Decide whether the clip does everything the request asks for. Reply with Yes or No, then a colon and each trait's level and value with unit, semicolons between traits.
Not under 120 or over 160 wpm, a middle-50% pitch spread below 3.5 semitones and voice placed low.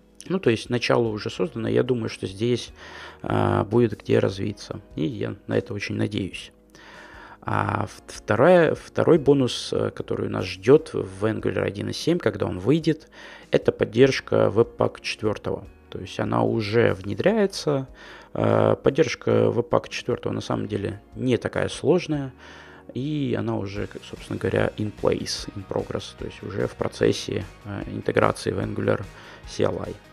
No: average, 135 wpm; average, 4.5 semitones; low, 115 Hz